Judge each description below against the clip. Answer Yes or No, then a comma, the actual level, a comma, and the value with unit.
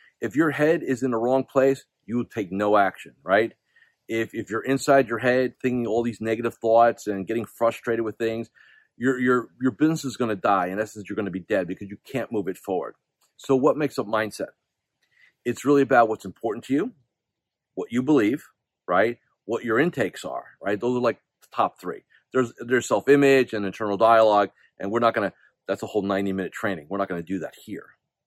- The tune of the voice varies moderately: Yes, average, 3.8 semitones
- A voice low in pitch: Yes, low, 115 Hz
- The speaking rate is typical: No, fast, 210 wpm